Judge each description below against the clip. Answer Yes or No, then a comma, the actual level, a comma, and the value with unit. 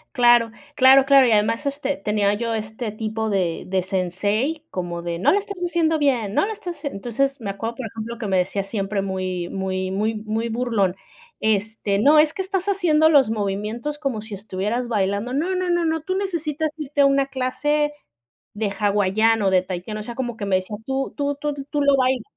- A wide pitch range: Yes, wide, 6.0 semitones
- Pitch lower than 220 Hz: No, high, 230 Hz